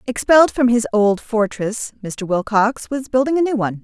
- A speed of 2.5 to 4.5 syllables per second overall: No, 5.1 syllables/s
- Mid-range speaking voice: No, high, 230 Hz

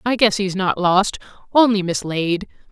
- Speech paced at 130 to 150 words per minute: Yes, slow, 135 wpm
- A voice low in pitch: No, high, 195 Hz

